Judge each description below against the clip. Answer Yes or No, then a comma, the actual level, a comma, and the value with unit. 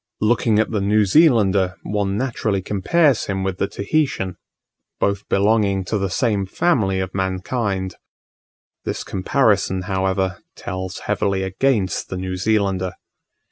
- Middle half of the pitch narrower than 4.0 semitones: Yes, narrow, 2.4 semitones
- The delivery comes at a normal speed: No, slow, 130 wpm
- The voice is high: No, low, 100 Hz